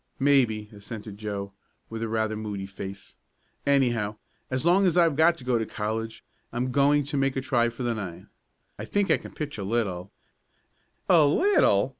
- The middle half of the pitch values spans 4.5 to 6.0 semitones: Yes, average, 5.0 semitones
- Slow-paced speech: No, average, 185 wpm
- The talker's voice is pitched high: No, low, 120 Hz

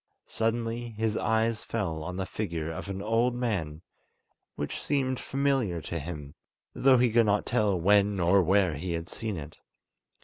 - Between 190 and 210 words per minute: No, average, 165 wpm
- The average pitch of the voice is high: No, low, 100 Hz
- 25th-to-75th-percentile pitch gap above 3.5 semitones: Yes, average, 5.3 semitones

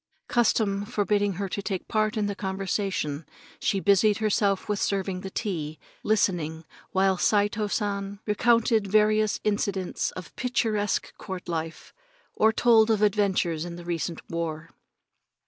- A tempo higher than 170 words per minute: No, average, 140 wpm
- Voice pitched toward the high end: Yes, high, 200 Hz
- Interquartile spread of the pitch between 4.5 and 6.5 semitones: No, narrow, 2.6 semitones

